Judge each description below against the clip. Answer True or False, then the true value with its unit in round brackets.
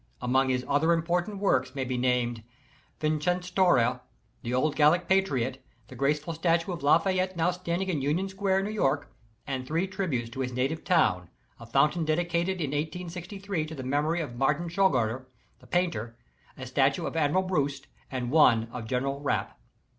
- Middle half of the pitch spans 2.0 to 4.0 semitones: False (5.4 semitones)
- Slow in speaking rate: False (165 wpm)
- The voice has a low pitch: False (155 Hz)